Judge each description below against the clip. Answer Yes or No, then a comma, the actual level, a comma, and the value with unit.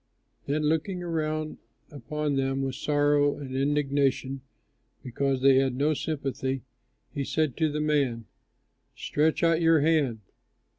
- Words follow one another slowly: Yes, slow, 130 wpm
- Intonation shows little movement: Yes, narrow, 2.3 semitones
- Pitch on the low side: No, medium, 145 Hz